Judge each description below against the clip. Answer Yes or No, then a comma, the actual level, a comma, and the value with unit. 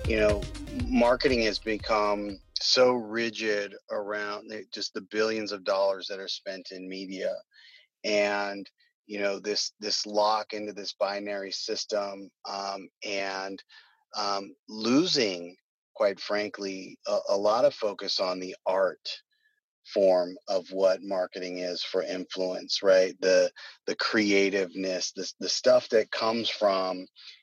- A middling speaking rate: No, slow, 130 wpm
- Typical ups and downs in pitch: No, narrow, 2.1 semitones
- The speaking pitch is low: Yes, low, 100 Hz